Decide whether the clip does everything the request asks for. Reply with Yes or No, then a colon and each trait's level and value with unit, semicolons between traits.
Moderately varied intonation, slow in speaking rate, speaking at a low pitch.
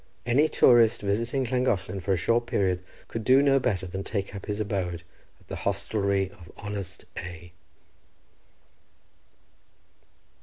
Yes: average, 3.9 semitones; slow, 130 wpm; low, 100 Hz